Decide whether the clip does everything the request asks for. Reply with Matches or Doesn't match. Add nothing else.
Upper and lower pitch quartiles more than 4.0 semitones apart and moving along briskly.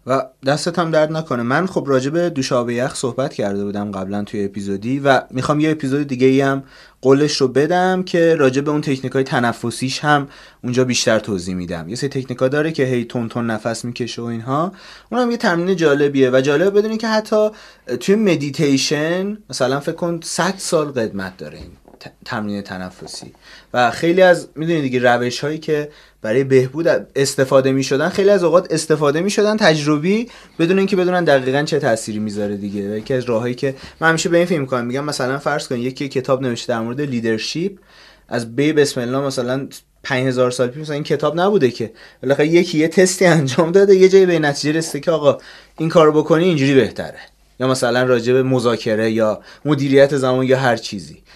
Matches